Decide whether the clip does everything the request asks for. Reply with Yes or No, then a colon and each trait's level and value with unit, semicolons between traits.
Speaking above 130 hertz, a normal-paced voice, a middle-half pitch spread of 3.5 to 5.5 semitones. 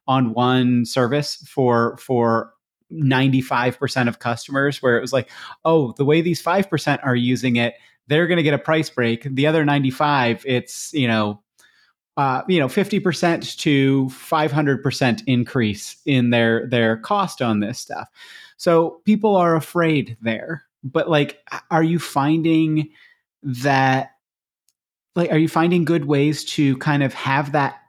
Yes: medium, 140 Hz; average, 165 wpm; average, 4.4 semitones